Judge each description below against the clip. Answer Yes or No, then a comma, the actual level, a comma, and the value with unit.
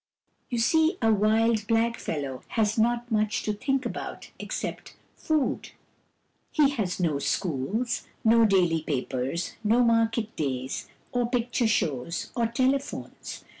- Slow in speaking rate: Yes, slow, 130 wpm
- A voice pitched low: No, high, 225 Hz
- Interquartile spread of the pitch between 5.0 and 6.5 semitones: Yes, wide, 5.4 semitones